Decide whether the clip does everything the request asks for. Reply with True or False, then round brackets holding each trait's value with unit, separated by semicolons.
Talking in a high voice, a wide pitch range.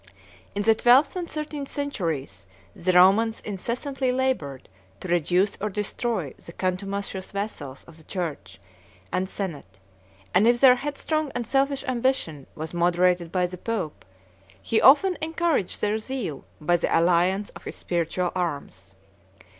True (195 Hz; 6.8 semitones)